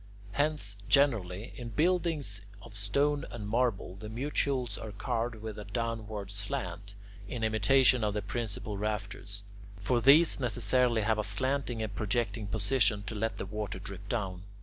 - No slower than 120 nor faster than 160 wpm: Yes, average, 150 wpm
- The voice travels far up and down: No, average, 3.3 semitones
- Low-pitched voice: Yes, low, 110 Hz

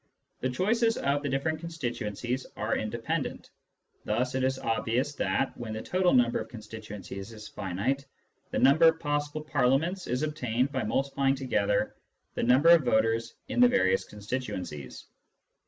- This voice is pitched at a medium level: No, low, 130 Hz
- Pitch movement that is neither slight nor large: Yes, average, 4.7 semitones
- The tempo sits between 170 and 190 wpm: No, average, 150 wpm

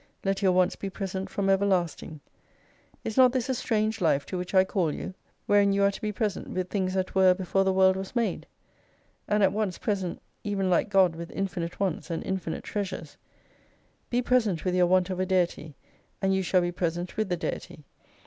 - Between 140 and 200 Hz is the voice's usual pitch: Yes, high, 190 Hz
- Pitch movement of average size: No, narrow, 1.9 semitones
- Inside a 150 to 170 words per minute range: No, fast, 205 wpm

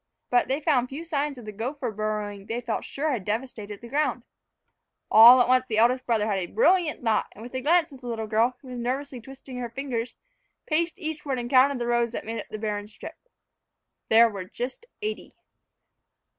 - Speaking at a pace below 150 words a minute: No, fast, 205 wpm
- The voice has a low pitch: No, high, 245 Hz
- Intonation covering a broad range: No, average, 3.8 semitones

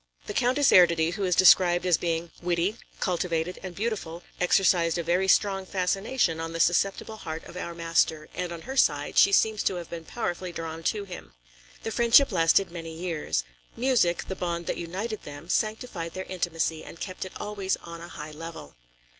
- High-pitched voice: No, medium, 175 Hz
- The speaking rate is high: No, average, 185 wpm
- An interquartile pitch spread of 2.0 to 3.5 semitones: Yes, average, 2.8 semitones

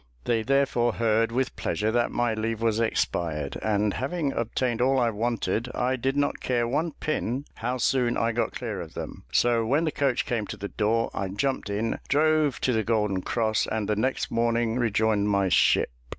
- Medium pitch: No, low, 115 Hz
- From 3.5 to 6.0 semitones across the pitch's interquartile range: No, average, 2.9 semitones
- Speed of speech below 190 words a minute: No, average, 195 wpm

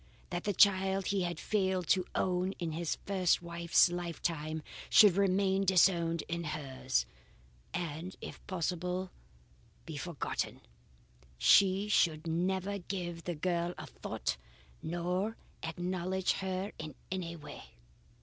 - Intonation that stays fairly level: Yes, narrow, 2.2 semitones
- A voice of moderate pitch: Yes, medium, 175 Hz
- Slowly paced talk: Yes, slow, 120 wpm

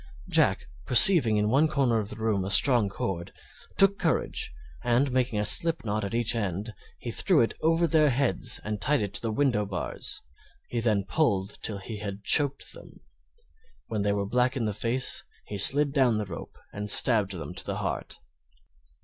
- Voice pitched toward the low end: Yes, low, 110 Hz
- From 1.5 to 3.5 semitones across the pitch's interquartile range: No, average, 4.7 semitones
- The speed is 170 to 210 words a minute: Yes, average, 190 wpm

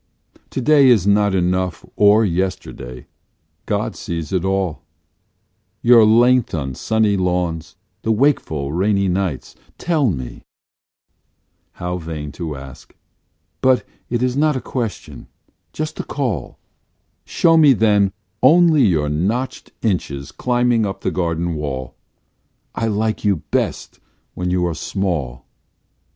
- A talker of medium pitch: No, very low, 95 Hz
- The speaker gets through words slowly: Yes, slow, 125 wpm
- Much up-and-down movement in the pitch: Yes, wide, 6.3 semitones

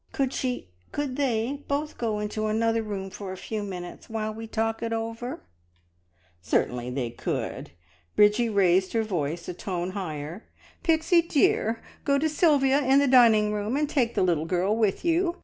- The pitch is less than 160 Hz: No, high, 220 Hz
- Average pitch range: No, wide, 5.9 semitones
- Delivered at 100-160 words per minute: No, average, 175 wpm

